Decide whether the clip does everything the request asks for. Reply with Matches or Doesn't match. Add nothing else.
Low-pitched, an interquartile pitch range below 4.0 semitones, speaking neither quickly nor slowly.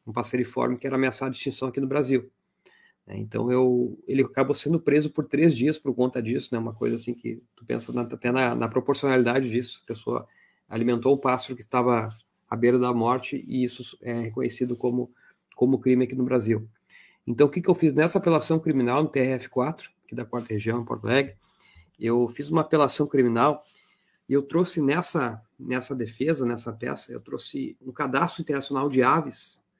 Doesn't match